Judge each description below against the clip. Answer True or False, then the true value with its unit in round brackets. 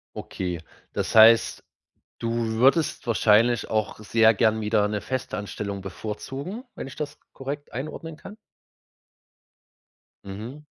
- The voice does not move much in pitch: False (4.5 semitones)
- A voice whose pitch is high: False (115 Hz)